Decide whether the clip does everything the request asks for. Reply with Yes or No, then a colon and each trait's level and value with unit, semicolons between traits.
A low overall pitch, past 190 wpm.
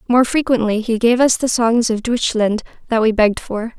No: high, 230 Hz; fast, 205 wpm